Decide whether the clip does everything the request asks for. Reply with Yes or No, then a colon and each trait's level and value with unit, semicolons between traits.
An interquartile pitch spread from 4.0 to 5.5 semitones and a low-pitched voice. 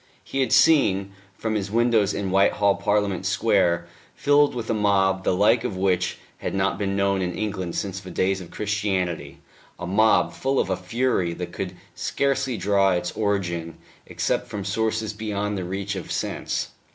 No: narrow, 2.6 semitones; low, 100 Hz